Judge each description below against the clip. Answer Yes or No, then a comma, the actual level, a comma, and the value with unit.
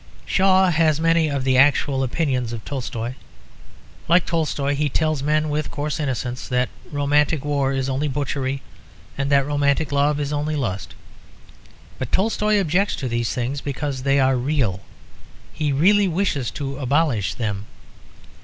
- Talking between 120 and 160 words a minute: Yes, average, 150 wpm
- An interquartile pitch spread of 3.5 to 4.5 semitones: No, average, 2.7 semitones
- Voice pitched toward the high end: No, medium, 140 Hz